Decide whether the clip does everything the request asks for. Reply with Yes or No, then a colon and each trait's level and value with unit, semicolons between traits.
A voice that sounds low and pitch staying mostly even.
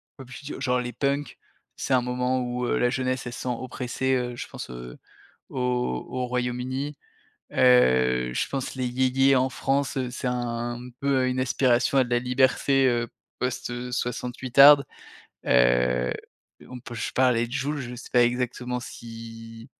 Yes: low, 125 Hz; narrow, 1.5 semitones